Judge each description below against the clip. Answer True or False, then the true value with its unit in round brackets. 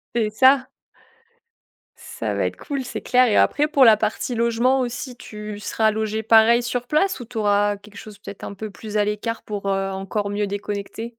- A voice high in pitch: True (220 Hz)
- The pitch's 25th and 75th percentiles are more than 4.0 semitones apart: False (2.9 semitones)